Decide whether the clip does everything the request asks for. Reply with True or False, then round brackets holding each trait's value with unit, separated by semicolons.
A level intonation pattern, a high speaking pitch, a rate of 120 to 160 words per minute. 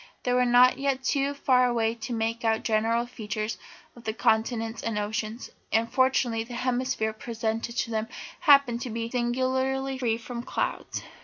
False (2.2 semitones; 235 Hz; 170 wpm)